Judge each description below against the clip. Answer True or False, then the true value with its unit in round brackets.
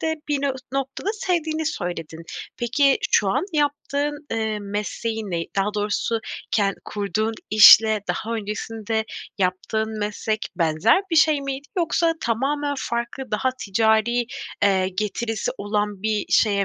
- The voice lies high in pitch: True (220 Hz)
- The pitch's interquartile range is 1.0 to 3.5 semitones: False (4.9 semitones)